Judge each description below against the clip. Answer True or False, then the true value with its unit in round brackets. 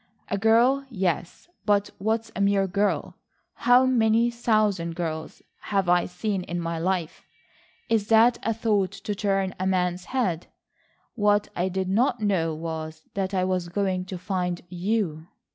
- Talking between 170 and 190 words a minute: False (155 wpm)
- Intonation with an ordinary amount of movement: True (3.5 semitones)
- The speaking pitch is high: True (195 Hz)